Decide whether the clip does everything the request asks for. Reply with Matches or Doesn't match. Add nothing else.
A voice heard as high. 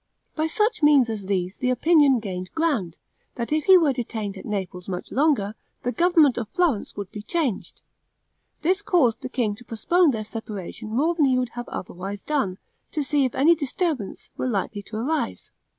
Matches